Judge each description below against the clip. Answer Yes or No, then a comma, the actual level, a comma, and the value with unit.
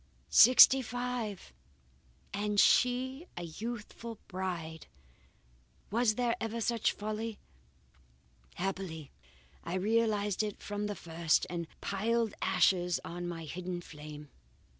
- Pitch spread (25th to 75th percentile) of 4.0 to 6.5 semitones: Yes, average, 4.7 semitones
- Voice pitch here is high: Yes, high, 205 Hz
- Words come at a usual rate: No, slow, 105 wpm